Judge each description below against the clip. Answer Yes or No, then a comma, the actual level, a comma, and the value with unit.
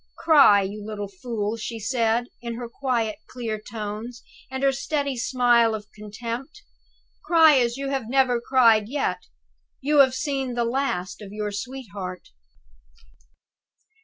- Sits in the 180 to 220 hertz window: No, high, 235 Hz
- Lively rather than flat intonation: No, average, 3.8 semitones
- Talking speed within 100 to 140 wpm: Yes, slow, 135 wpm